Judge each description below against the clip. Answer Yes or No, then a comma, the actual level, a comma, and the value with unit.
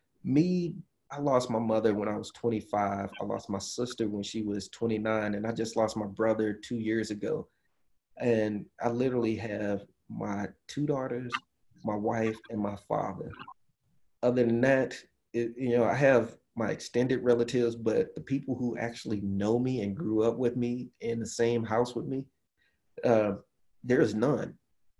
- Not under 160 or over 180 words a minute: Yes, average, 170 wpm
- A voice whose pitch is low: Yes, low, 115 Hz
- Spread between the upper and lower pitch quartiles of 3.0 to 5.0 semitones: No, narrow, 2.6 semitones